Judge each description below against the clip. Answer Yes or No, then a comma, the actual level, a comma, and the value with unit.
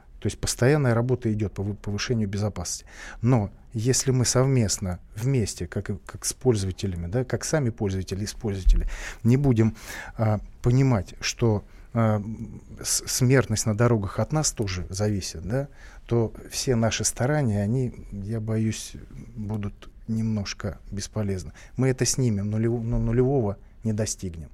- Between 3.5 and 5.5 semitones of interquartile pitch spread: No, average, 3.1 semitones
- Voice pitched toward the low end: Yes, low, 110 Hz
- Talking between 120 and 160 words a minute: Yes, average, 130 wpm